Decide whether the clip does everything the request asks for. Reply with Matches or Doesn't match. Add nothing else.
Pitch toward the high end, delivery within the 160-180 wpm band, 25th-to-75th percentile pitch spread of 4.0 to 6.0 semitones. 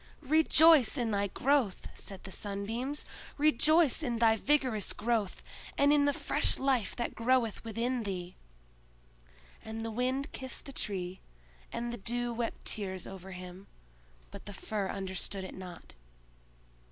Doesn't match